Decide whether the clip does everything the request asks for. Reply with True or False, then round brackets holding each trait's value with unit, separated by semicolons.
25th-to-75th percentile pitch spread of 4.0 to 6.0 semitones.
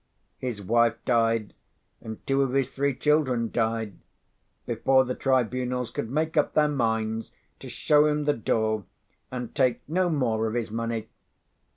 False (3.4 semitones)